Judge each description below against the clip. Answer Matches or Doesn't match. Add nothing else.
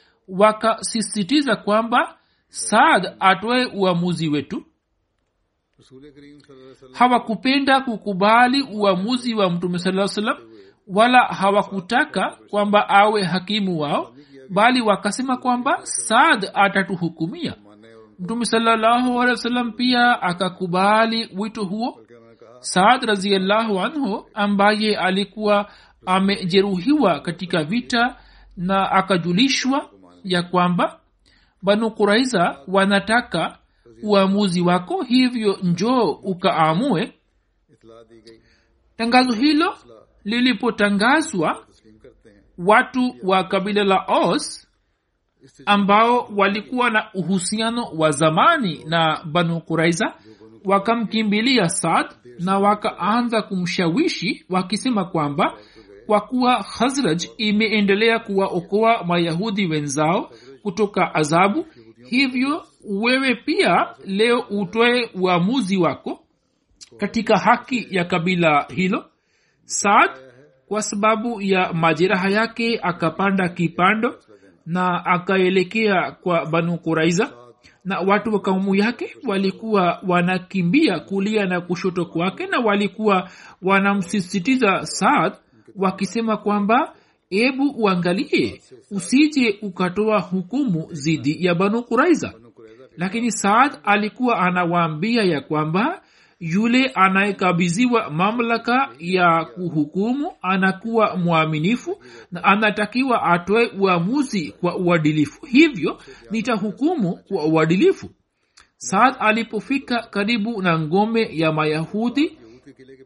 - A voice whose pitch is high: Matches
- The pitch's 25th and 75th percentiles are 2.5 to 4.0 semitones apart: Doesn't match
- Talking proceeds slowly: Matches